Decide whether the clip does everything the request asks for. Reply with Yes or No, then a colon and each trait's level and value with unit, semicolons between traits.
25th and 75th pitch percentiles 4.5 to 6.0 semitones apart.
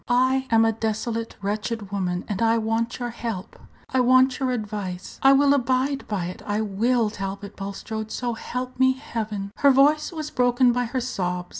No: average, 3.7 semitones